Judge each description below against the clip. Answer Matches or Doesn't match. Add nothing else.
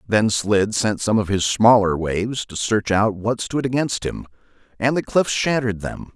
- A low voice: Matches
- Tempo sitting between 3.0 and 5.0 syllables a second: Matches